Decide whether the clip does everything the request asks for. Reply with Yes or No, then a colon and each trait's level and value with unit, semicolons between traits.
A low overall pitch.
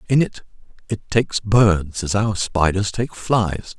Yes: low, 100 Hz